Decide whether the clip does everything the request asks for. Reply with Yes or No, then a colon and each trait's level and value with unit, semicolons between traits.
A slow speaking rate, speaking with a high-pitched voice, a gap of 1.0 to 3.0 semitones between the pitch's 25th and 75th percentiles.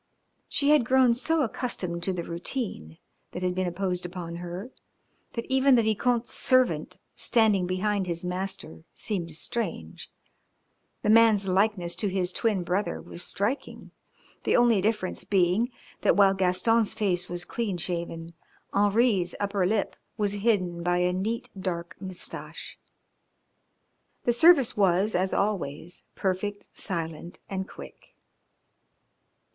No: slow, 130 wpm; high, 195 Hz; average, 3.9 semitones